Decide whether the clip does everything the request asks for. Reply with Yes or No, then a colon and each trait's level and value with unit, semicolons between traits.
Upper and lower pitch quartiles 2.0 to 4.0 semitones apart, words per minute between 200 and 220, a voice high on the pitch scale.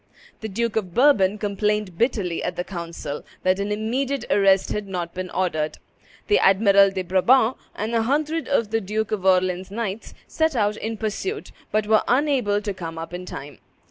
No: average, 3.5 semitones; average, 180 wpm; high, 205 Hz